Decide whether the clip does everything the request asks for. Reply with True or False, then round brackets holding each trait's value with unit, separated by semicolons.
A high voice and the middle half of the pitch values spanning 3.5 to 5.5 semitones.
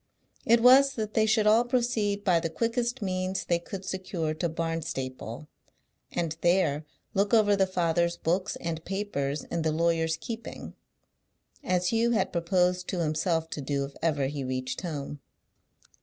False (175 Hz; 4.4 semitones)